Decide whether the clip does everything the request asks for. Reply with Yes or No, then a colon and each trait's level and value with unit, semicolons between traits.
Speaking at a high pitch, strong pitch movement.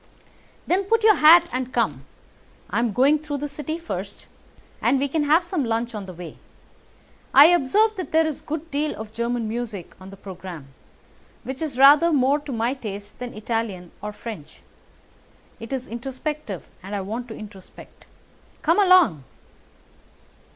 Yes: very high, 255 Hz; wide, 6.3 semitones